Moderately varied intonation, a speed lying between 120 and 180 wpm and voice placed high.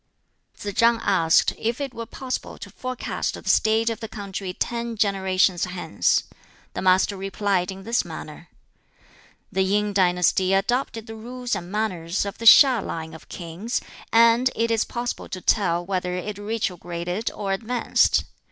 Yes: average, 3.8 semitones; average, 155 wpm; high, 205 Hz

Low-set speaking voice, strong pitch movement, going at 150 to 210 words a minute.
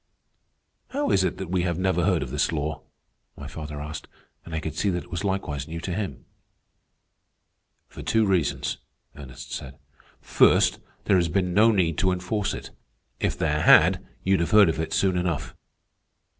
No: very low, 90 Hz; average, 3.3 semitones; average, 180 wpm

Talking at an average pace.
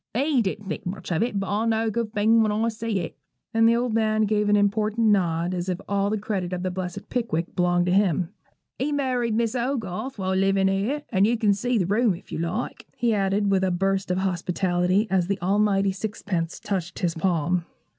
No: fast, 220 wpm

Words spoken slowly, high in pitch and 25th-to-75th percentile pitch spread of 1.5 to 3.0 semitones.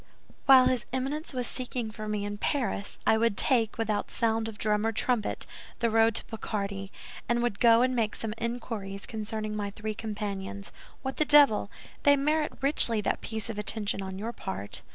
No: average, 185 wpm; high, 225 Hz; average, 2.7 semitones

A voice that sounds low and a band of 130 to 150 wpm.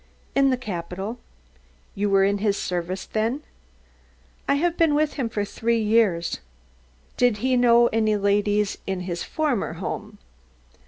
No: high, 215 Hz; average, 145 wpm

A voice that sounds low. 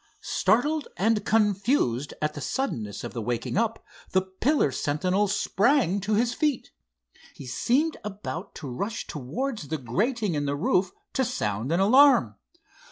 No: high, 200 Hz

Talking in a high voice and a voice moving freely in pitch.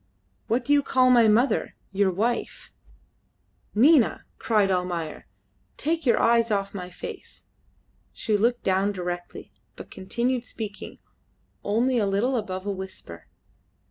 No: high, 210 Hz; average, 4.1 semitones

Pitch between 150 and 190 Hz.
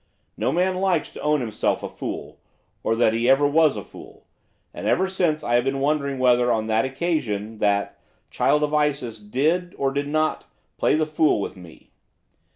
No: medium, 140 Hz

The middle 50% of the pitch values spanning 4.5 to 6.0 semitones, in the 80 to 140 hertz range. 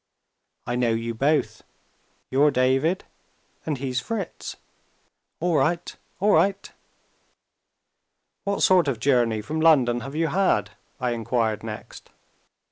Yes: wide, 5.6 semitones; low, 135 Hz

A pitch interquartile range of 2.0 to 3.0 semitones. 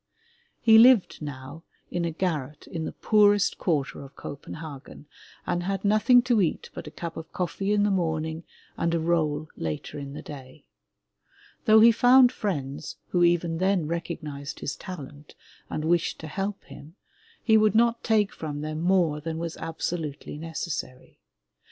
No: average, 4.8 semitones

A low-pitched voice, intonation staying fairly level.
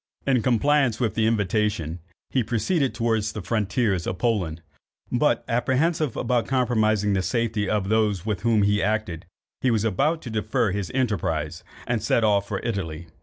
No: low, 110 Hz; average, 3.2 semitones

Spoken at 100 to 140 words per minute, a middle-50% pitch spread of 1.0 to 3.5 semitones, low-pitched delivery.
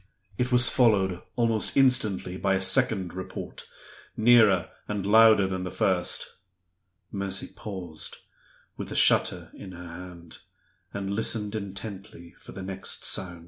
Yes: slow, 135 wpm; average, 3.0 semitones; very low, 95 Hz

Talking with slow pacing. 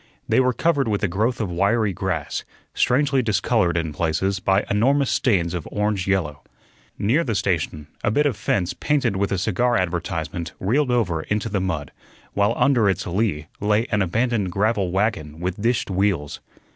No: average, 170 wpm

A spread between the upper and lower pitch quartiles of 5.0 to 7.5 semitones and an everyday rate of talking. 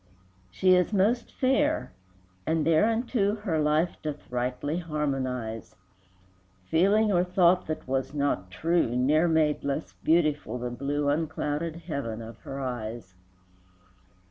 No: wide, 5.4 semitones; slow, 125 wpm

